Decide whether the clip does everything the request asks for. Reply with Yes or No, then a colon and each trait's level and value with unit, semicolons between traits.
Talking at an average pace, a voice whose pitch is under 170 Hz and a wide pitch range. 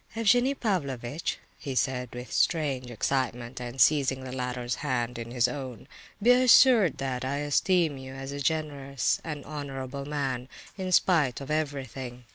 No: average, 150 wpm; low, 135 Hz; average, 3.4 semitones